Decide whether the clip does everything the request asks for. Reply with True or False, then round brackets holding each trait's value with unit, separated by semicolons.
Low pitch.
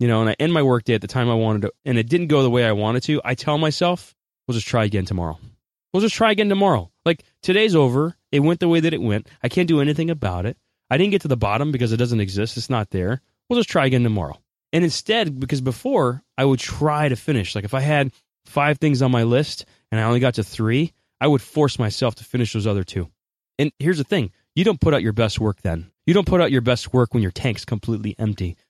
True (125 Hz)